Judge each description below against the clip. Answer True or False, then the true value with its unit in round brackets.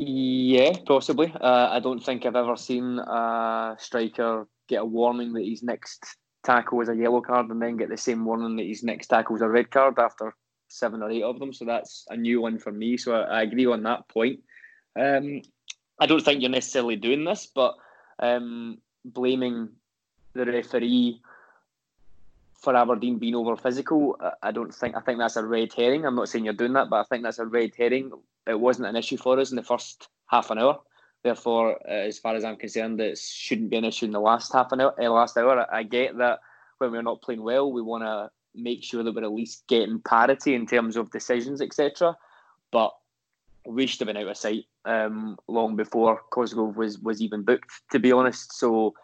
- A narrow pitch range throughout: True (1.9 semitones)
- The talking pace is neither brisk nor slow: False (210 wpm)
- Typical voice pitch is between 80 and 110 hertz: False (120 Hz)